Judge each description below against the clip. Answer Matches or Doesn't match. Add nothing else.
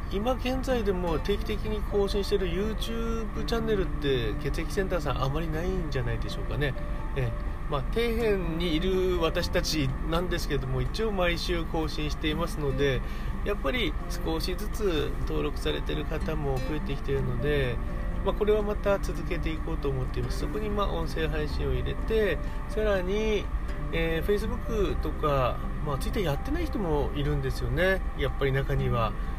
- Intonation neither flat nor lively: Doesn't match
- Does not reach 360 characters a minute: Doesn't match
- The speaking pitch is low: Doesn't match